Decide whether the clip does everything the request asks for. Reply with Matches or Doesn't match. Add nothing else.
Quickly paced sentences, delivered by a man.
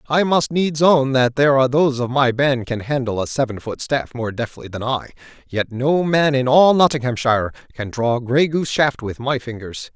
Matches